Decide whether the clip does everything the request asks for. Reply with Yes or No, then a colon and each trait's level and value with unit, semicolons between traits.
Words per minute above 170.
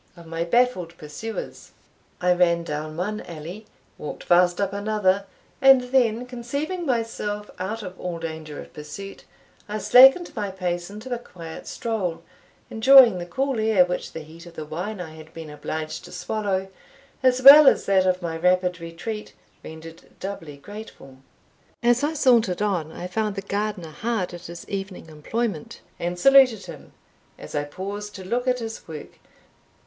No: average, 165 wpm